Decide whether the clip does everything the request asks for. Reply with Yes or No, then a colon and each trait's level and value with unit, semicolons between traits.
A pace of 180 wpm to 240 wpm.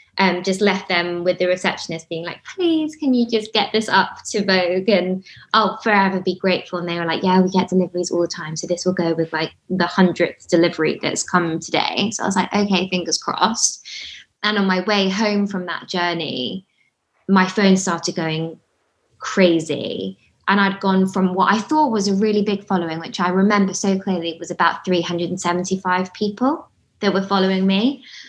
Yes: average, 195 wpm